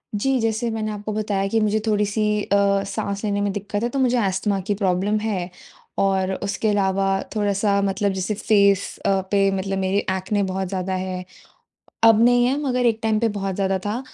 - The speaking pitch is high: Yes, high, 200 Hz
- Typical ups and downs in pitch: No, narrow, 2.0 semitones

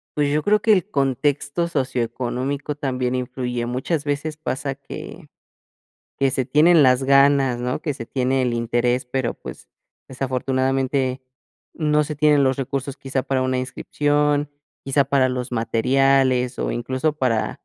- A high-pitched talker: No, low, 135 Hz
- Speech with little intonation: Yes, narrow, 2.2 semitones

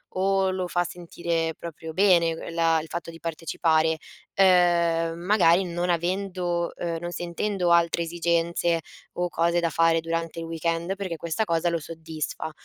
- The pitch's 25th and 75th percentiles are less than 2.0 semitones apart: Yes, narrow, 1.2 semitones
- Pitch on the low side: No, medium, 170 Hz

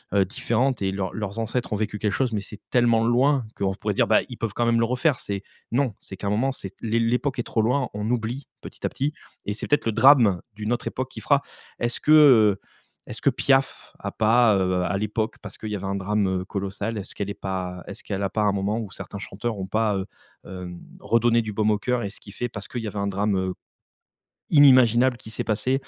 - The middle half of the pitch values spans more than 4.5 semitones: No, average, 3.3 semitones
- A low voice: Yes, low, 110 Hz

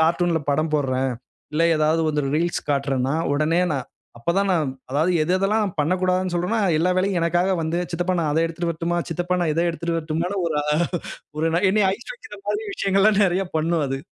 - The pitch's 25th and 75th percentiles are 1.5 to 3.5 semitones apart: Yes, average, 2.9 semitones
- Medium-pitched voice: Yes, medium, 170 Hz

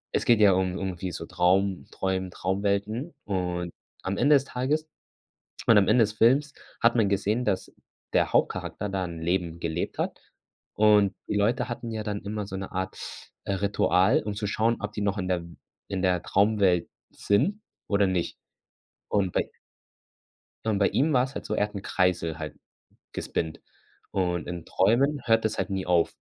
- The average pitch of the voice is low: Yes, low, 100 Hz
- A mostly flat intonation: No, average, 3.0 semitones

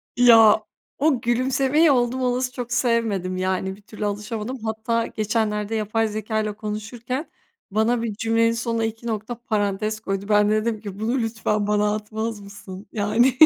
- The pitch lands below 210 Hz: No, high, 220 Hz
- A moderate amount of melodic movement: No, narrow, 2.1 semitones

